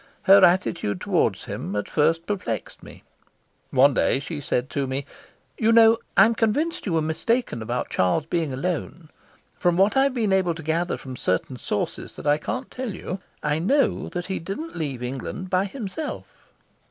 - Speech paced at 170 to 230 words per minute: Yes, average, 175 wpm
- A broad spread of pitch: Yes, wide, 6.8 semitones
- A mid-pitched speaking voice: Yes, medium, 175 Hz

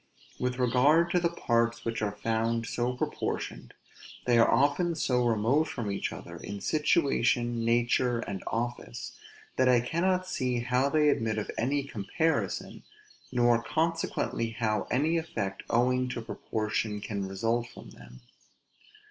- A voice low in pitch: Yes, low, 120 Hz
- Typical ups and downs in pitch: Yes, average, 3.7 semitones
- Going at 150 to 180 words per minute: No, average, 140 wpm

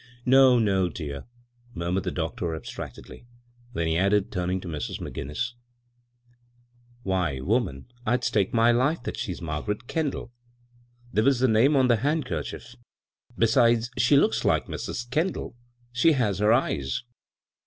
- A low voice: Yes, low, 115 Hz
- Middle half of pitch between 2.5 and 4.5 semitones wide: No, average, 5.2 semitones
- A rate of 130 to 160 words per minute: Yes, average, 145 wpm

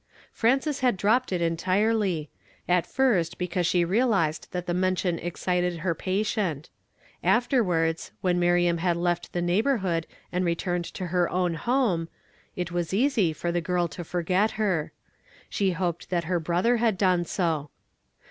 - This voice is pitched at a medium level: Yes, medium, 180 Hz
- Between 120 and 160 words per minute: Yes, average, 150 wpm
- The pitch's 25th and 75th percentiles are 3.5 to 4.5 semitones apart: No, average, 2.7 semitones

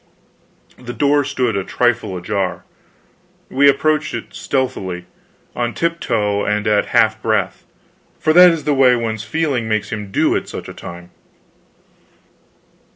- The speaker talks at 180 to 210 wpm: No, average, 140 wpm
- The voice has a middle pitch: No, low, 115 Hz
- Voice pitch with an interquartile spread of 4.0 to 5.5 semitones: Yes, average, 5.2 semitones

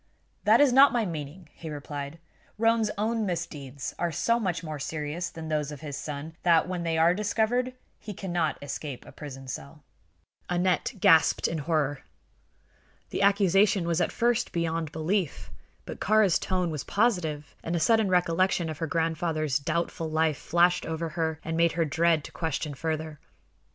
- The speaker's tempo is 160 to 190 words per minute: Yes, average, 165 wpm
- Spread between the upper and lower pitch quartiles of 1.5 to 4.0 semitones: Yes, average, 3.4 semitones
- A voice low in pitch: No, medium, 165 Hz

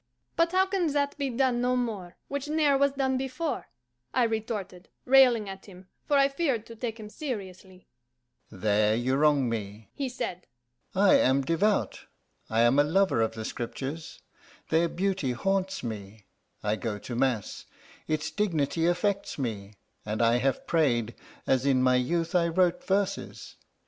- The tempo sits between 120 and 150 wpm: No, average, 160 wpm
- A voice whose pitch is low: No, medium, 180 Hz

